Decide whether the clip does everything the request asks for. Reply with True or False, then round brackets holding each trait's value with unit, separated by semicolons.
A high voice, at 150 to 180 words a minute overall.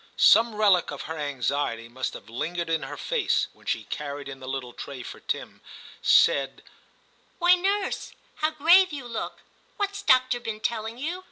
True (215 Hz; 170 wpm)